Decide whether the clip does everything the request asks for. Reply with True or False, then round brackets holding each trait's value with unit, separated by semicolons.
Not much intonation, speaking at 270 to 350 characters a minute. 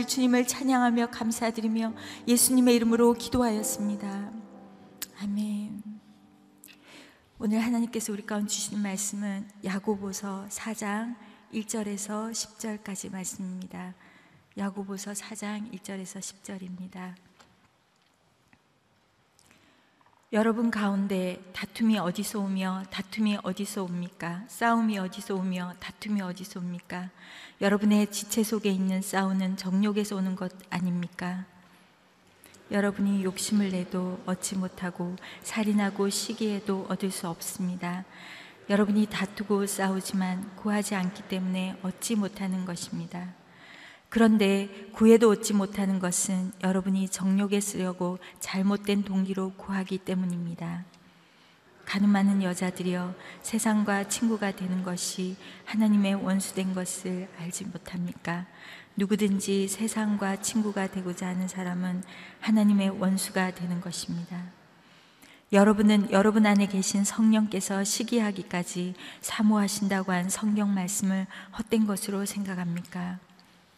True (2.2 semitones; 275 characters per minute)